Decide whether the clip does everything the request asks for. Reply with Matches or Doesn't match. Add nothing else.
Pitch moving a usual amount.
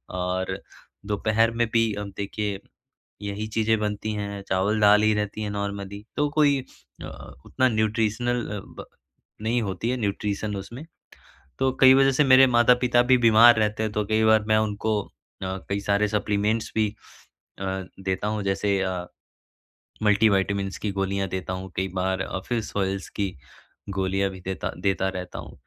Doesn't match